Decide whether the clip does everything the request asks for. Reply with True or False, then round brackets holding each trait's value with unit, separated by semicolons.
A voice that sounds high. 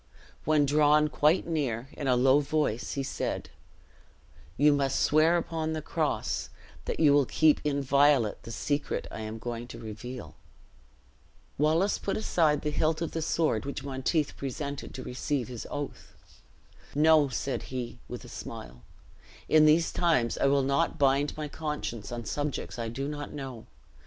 False (145 Hz)